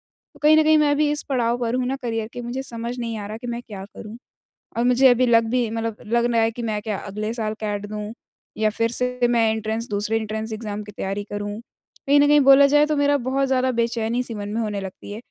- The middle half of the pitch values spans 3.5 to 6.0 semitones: No, average, 2.9 semitones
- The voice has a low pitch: No, high, 230 Hz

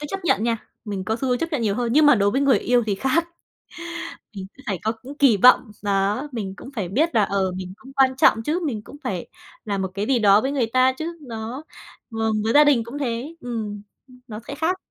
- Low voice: No, high, 235 Hz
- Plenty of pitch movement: No, average, 4.8 semitones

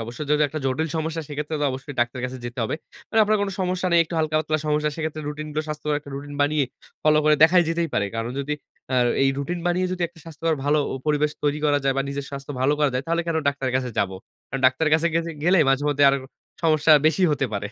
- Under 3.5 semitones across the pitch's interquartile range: Yes, narrow, 2.6 semitones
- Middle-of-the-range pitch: Yes, medium, 150 Hz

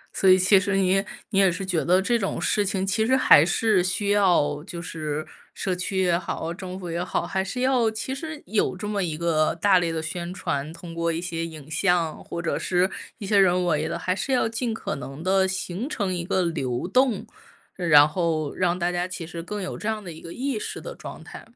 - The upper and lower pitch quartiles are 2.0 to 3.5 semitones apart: Yes, average, 3.1 semitones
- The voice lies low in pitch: No, medium, 185 Hz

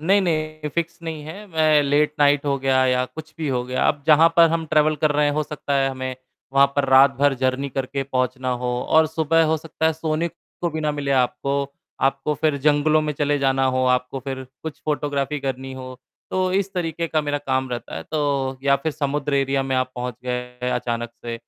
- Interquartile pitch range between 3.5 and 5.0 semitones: No, average, 2.8 semitones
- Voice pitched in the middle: Yes, medium, 145 Hz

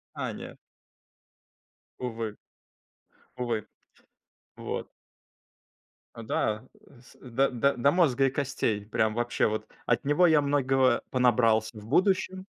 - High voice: No, low, 125 Hz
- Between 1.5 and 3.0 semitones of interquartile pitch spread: No, average, 3.8 semitones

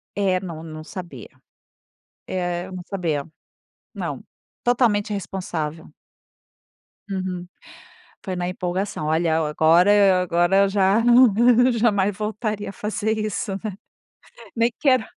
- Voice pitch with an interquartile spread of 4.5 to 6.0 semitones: No, average, 3.2 semitones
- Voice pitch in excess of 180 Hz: Yes, high, 190 Hz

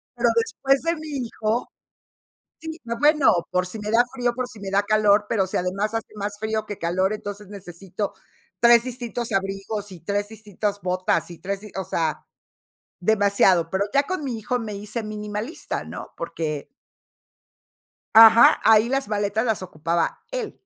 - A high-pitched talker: Yes, high, 210 Hz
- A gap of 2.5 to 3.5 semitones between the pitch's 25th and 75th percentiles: Yes, average, 3.1 semitones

